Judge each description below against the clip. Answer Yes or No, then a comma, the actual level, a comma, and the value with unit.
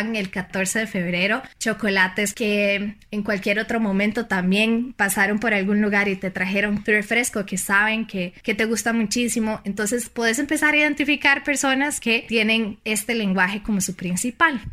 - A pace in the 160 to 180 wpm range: Yes, average, 165 wpm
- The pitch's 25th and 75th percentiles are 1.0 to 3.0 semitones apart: Yes, narrow, 2.6 semitones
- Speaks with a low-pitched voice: No, high, 215 Hz